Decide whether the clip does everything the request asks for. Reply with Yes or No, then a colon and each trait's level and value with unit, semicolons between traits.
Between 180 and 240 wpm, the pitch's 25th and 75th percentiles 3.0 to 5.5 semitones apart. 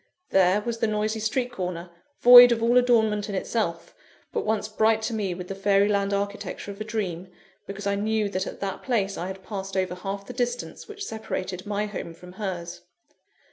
No: average, 200 wpm; narrow, 2.6 semitones